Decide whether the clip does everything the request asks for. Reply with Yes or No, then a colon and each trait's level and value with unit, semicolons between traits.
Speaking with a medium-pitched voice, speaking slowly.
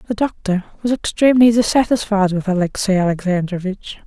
No: high, 205 Hz; slow, 120 wpm